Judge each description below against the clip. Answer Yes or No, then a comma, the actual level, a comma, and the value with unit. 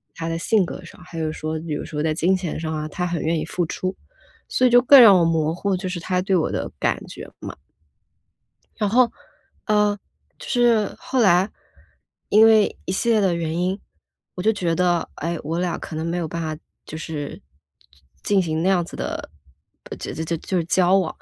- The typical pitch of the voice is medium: Yes, medium, 175 Hz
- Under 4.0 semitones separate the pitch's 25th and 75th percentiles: Yes, average, 3.6 semitones